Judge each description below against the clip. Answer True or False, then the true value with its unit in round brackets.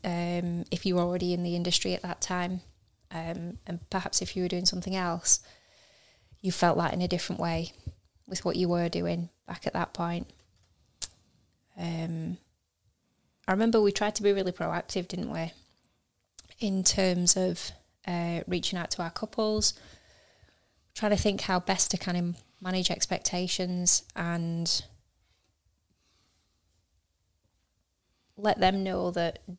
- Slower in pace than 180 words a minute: True (145 wpm)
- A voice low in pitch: False (175 Hz)